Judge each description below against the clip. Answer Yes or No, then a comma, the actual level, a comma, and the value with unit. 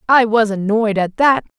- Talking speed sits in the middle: Yes, average, 190 wpm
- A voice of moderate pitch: No, high, 220 Hz